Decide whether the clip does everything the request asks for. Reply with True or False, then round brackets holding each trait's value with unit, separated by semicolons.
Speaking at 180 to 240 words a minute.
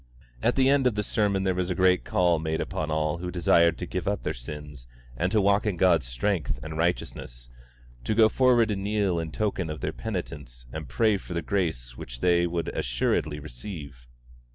True (200 wpm)